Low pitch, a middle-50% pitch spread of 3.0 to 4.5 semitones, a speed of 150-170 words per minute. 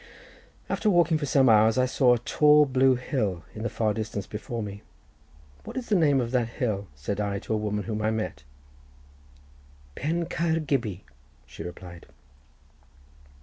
No: low, 115 Hz; average, 5.1 semitones; average, 165 wpm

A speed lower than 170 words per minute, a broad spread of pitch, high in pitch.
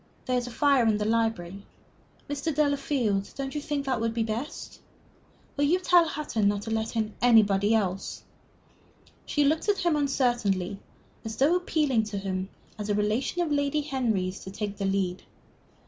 No: average, 175 wpm; wide, 5.7 semitones; high, 230 Hz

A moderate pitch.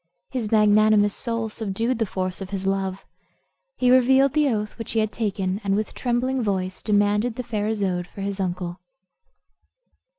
No: high, 210 Hz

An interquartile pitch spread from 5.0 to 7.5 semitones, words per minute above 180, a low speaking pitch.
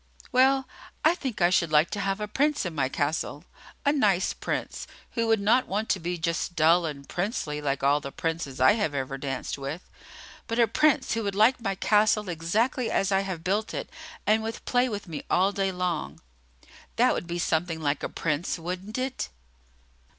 No: wide, 5.5 semitones; average, 195 wpm; medium, 185 Hz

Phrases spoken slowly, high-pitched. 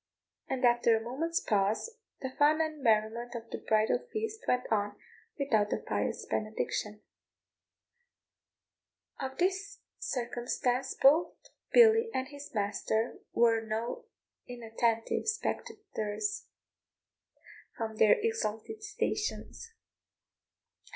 Yes: slow, 100 wpm; high, 245 Hz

